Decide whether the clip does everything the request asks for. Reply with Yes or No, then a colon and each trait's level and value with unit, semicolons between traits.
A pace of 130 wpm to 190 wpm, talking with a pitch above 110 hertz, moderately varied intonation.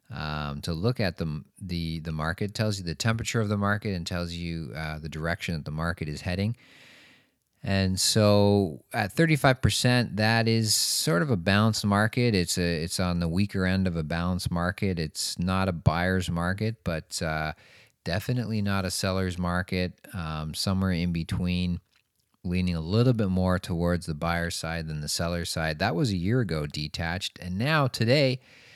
No: average, 185 wpm; very low, 90 Hz; average, 4.2 semitones